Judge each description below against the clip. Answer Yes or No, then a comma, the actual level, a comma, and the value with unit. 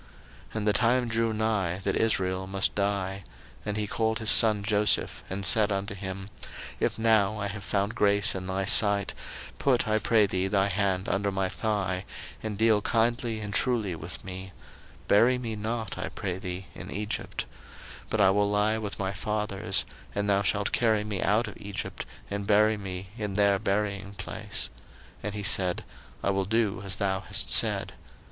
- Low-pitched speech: Yes, low, 100 Hz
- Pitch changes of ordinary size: No, narrow, 2.0 semitones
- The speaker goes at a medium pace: Yes, average, 180 wpm